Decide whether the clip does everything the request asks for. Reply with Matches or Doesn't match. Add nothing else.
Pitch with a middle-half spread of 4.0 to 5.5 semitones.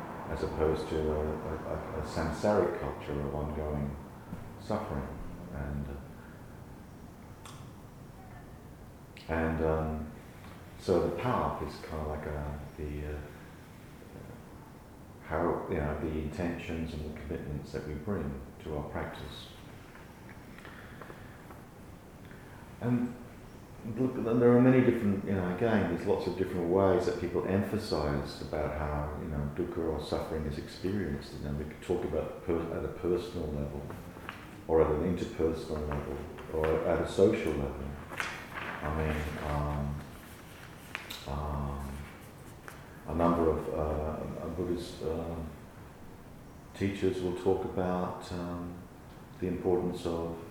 Doesn't match